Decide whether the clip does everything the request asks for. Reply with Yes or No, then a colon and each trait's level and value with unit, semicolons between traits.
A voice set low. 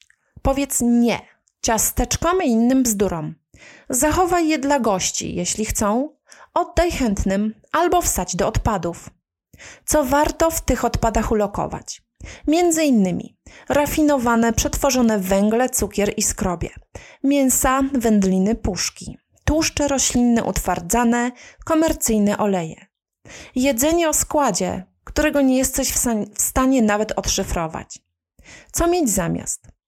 No: high, 240 Hz